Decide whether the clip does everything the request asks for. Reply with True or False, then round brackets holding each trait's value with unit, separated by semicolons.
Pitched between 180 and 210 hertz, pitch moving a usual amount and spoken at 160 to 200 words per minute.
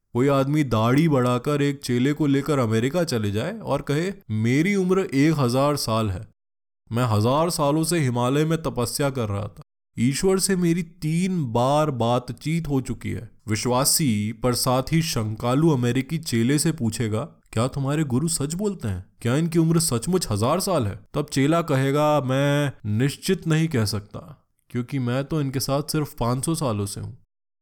False (135 Hz; 4.6 semitones; 170 wpm)